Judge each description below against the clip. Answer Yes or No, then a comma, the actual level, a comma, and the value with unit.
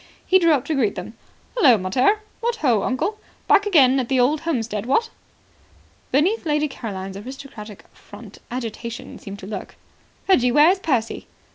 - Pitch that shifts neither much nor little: No, wide, 6.4 semitones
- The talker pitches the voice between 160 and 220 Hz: No, very high, 260 Hz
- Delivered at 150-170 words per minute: Yes, average, 160 wpm